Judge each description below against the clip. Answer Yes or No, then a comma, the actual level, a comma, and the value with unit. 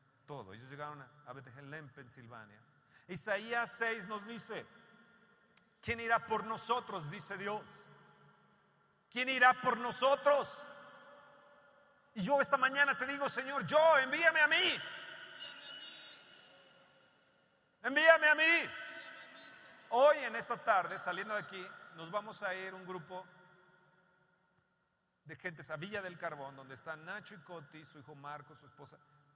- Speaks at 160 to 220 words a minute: No, average, 130 wpm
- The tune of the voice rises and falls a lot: Yes, wide, 7.9 semitones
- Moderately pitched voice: No, high, 200 Hz